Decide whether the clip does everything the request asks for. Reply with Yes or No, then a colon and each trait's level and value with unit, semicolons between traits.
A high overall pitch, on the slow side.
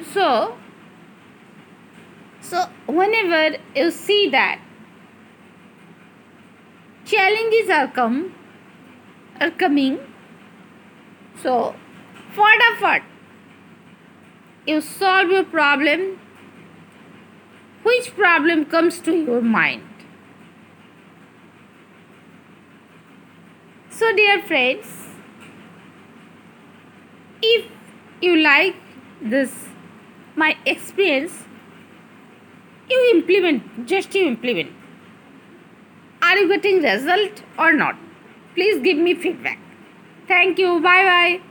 Yes: very high, 345 Hz; slow, 75 wpm